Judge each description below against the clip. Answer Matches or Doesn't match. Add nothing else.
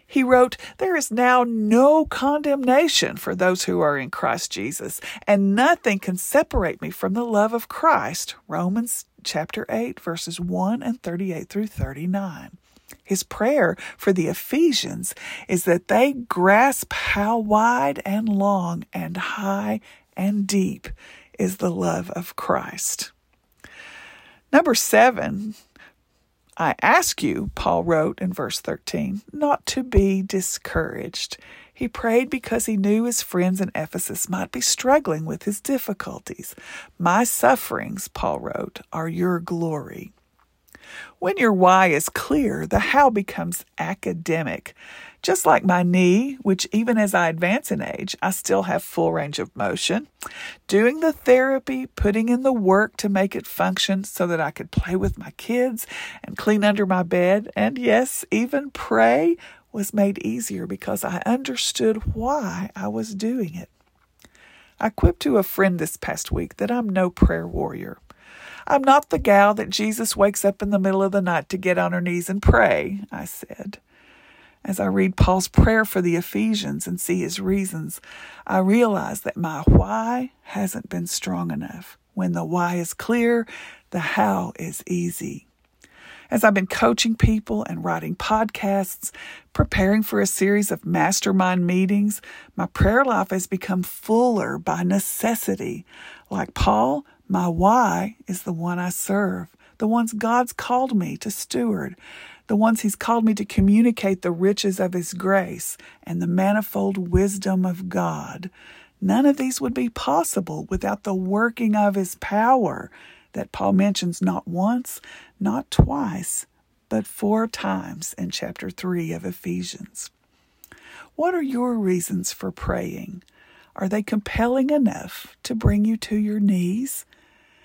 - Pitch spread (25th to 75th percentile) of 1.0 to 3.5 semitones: Doesn't match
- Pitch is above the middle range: Matches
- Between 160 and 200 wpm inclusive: Doesn't match